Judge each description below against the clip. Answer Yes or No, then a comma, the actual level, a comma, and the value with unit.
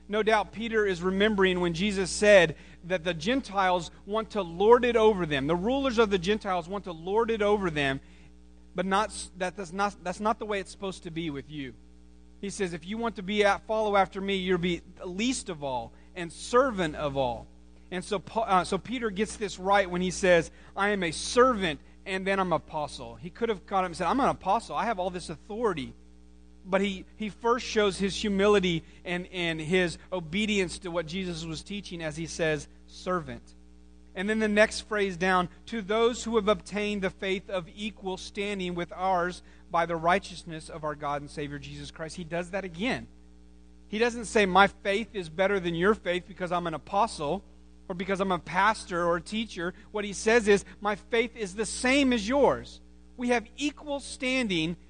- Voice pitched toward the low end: No, medium, 185 Hz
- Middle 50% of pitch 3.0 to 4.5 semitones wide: Yes, average, 4.1 semitones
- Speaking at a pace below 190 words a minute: No, fast, 205 wpm